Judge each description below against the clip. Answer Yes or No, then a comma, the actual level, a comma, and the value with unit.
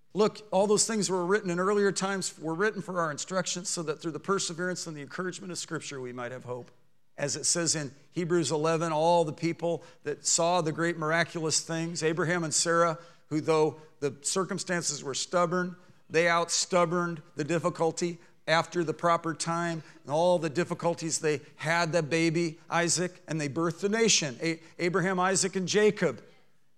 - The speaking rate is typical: Yes, average, 170 wpm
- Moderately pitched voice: Yes, medium, 170 Hz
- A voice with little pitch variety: Yes, narrow, 2.1 semitones